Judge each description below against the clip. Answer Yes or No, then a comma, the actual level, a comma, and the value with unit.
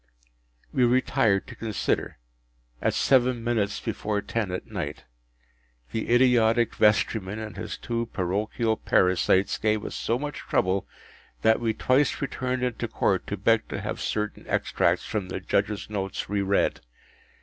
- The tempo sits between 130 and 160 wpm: Yes, average, 145 wpm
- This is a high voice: No, low, 110 Hz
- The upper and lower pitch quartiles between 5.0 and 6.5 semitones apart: No, average, 3.2 semitones